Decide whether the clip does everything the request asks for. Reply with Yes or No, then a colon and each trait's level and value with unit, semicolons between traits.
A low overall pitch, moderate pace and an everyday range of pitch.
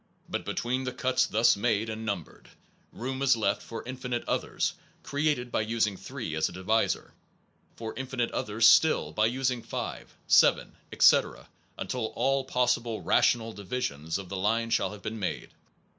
Yes: low, 115 Hz; average, 160 wpm; average, 3.2 semitones